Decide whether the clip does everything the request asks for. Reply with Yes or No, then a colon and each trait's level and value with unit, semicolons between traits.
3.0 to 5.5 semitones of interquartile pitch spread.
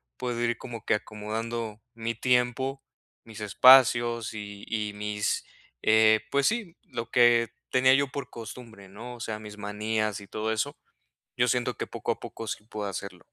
No: narrow, 2.6 semitones